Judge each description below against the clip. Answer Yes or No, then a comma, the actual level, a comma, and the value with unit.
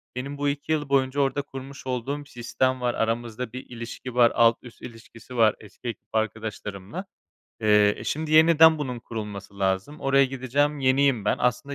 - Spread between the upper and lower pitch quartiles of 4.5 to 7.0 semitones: No, average, 3.7 semitones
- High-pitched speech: No, low, 125 Hz